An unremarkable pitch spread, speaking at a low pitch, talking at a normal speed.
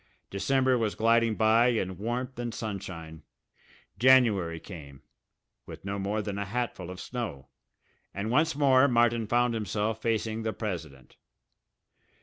No: average, 3.5 semitones; low, 110 Hz; slow, 130 wpm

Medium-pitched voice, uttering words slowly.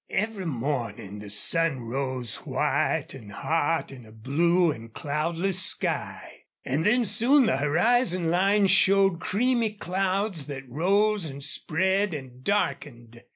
Yes: medium, 165 Hz; slow, 130 wpm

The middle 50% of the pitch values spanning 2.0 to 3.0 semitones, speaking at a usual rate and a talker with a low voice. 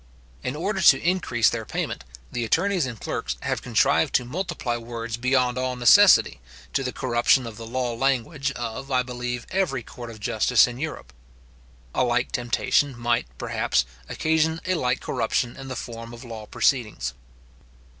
Yes: average, 2.7 semitones; average, 165 wpm; low, 125 Hz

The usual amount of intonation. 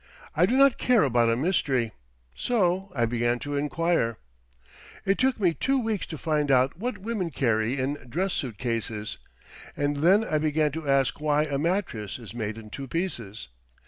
No: wide, 7.0 semitones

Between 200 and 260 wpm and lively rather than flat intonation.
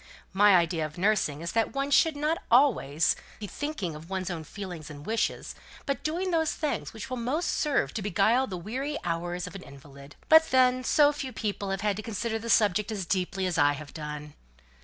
Yes: fast, 205 wpm; wide, 7.3 semitones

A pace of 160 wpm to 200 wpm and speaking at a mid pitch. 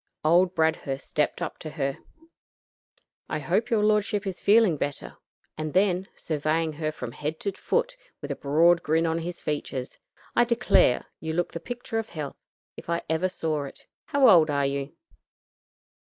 Yes: average, 170 wpm; medium, 165 Hz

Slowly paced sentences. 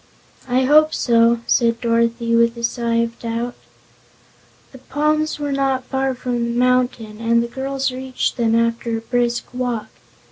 No: average, 155 wpm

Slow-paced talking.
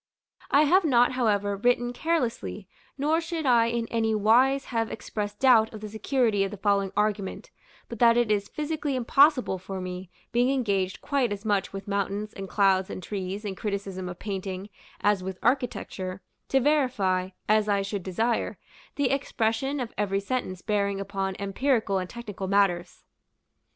No: average, 165 wpm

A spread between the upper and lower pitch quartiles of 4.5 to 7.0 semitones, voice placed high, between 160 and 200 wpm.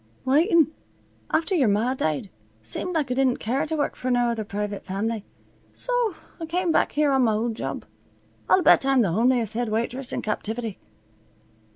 Yes: wide, 5.6 semitones; high, 245 Hz; average, 180 wpm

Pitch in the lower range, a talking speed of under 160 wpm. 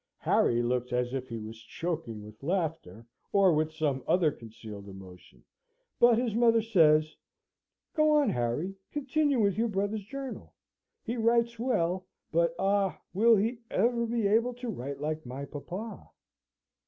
No: medium, 180 Hz; average, 150 wpm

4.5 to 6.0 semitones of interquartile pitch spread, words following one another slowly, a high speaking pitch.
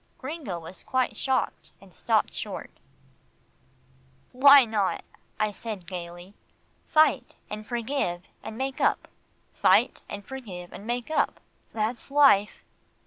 Yes: wide, 5.6 semitones; slow, 120 wpm; high, 220 Hz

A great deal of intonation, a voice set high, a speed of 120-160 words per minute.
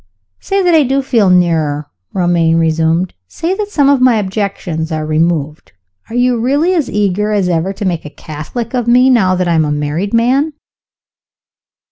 No: wide, 7.5 semitones; high, 195 Hz; average, 180 wpm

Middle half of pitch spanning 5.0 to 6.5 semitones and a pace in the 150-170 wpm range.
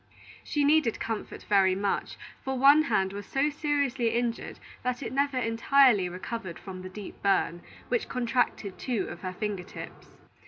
Yes: wide, 5.6 semitones; average, 160 wpm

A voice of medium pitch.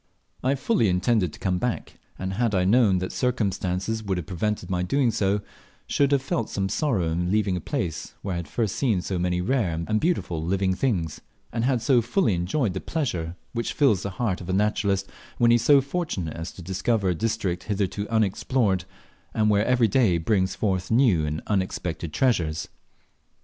No: low, 100 Hz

